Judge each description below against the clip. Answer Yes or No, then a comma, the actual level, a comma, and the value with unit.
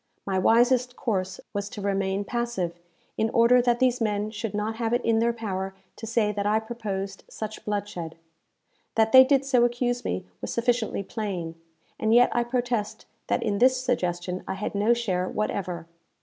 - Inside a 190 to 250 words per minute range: No, average, 175 wpm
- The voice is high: Yes, high, 220 Hz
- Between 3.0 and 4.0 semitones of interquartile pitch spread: Yes, average, 3.4 semitones